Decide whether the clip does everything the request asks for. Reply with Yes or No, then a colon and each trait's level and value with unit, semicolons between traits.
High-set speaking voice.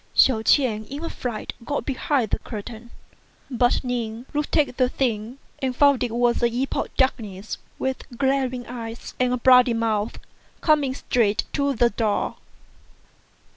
Yes: high, 245 Hz